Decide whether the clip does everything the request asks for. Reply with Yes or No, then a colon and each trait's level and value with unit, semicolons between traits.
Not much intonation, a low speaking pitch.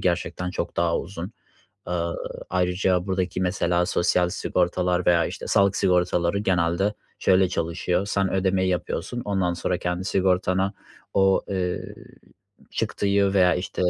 Yes: narrow, 1.4 semitones; very low, 90 Hz